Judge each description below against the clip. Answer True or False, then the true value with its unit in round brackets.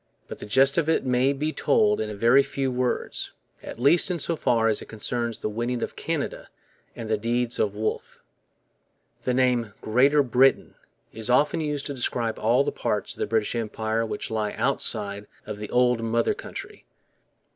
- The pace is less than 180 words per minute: False (185 wpm)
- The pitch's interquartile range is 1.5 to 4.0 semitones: True (3.5 semitones)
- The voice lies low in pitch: True (120 Hz)